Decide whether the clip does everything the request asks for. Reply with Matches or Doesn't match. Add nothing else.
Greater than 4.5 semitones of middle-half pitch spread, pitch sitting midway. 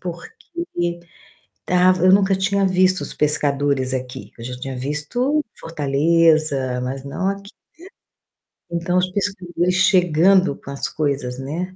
Matches